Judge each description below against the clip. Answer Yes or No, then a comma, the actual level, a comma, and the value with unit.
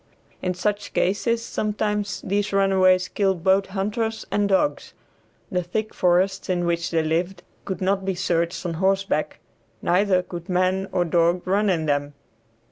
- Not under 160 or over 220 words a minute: No, average, 150 wpm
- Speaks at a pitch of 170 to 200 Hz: Yes, high, 190 Hz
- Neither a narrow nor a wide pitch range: No, narrow, 2.2 semitones